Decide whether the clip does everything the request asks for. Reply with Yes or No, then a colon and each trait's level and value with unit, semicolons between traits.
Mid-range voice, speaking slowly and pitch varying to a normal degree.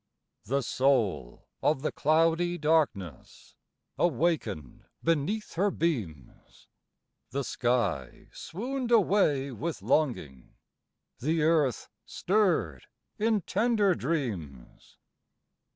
No: medium, 150 Hz; slow, 85 wpm; wide, 7.5 semitones